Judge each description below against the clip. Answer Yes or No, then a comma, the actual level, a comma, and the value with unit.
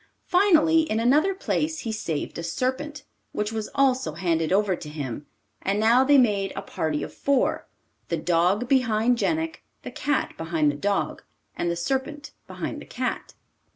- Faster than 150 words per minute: Yes, average, 165 wpm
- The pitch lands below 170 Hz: No, high, 220 Hz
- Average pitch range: No, wide, 8.6 semitones